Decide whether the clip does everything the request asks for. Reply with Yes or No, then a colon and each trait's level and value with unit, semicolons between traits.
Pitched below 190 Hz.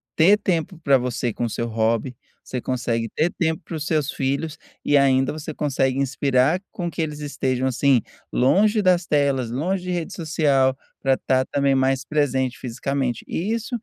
Yes: medium, 140 Hz